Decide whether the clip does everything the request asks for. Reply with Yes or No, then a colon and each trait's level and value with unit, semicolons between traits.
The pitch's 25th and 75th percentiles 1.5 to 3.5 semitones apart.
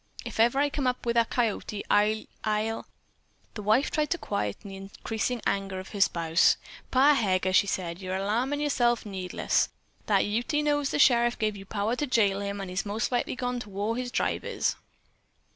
No: average, 3.9 semitones